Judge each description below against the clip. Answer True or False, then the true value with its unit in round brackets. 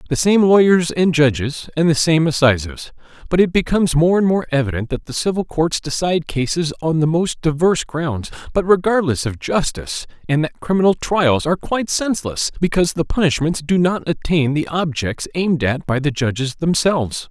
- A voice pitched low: False (160 Hz)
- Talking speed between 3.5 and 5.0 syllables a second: False (5.4 syllables/s)